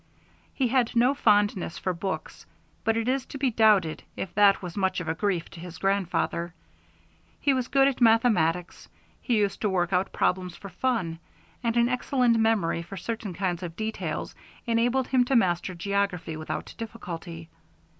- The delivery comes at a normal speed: Yes, average, 170 wpm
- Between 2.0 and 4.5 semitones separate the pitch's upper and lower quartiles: No, average, 4.9 semitones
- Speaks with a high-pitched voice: Yes, high, 200 Hz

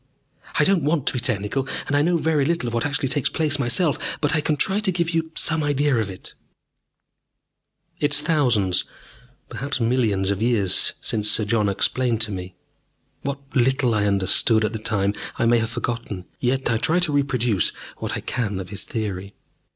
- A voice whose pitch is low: Yes, low, 120 Hz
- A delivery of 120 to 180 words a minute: No, average, 190 wpm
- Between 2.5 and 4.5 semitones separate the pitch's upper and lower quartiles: No, wide, 5.5 semitones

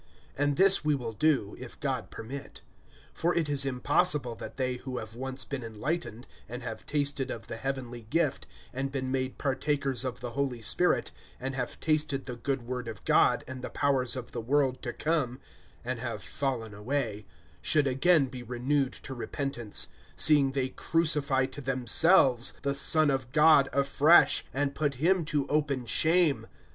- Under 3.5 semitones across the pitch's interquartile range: Yes, average, 2.7 semitones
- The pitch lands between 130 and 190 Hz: Yes, low, 135 Hz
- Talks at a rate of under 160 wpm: No, average, 170 wpm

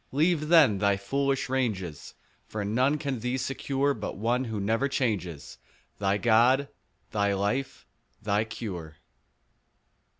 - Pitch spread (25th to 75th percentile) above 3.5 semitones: Yes, average, 5.0 semitones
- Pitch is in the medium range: No, low, 115 Hz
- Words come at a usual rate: No, slow, 125 wpm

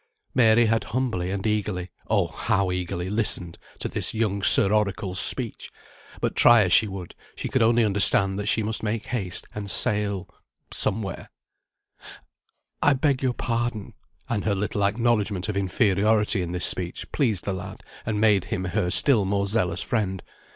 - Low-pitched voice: Yes, low, 105 Hz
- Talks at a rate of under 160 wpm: No, average, 165 wpm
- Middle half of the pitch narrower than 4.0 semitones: Yes, average, 2.9 semitones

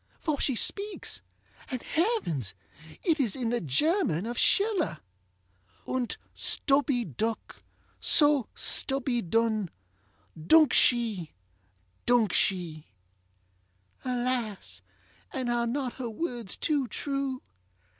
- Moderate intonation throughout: No, wide, 8.5 semitones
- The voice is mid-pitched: No, high, 240 Hz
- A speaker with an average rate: No, slow, 100 wpm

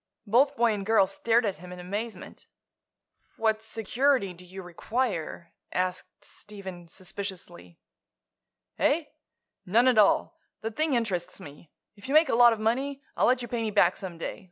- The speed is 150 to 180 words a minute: Yes, average, 165 wpm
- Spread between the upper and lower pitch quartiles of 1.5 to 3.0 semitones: No, average, 4.6 semitones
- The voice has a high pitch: Yes, high, 210 Hz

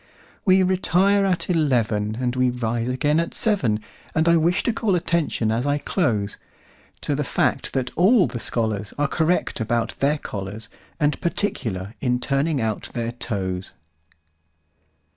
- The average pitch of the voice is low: Yes, low, 130 Hz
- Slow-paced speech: Yes, slow, 130 wpm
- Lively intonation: Yes, wide, 7.1 semitones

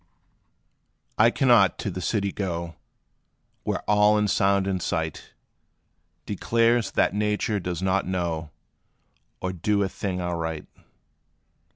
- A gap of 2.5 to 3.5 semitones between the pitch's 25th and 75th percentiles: Yes, average, 3.0 semitones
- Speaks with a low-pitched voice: Yes, very low, 95 Hz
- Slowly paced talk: Yes, slow, 115 wpm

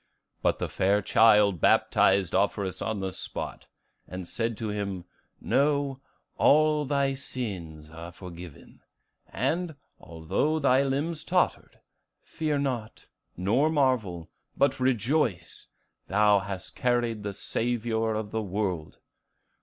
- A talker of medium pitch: No, low, 110 Hz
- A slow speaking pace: Yes, slow, 115 wpm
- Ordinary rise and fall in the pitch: No, wide, 6.1 semitones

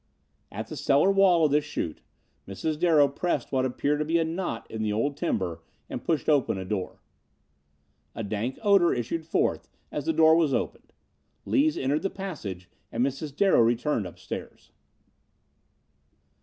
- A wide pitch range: Yes, wide, 6.5 semitones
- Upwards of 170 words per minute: No, average, 160 wpm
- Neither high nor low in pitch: Yes, medium, 145 Hz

